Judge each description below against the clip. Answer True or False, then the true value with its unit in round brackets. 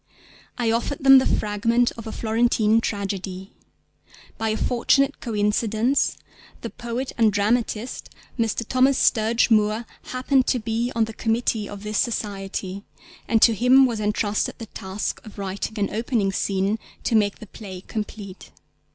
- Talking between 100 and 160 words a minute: True (150 wpm)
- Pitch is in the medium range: False (220 Hz)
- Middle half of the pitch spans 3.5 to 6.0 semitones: False (2.5 semitones)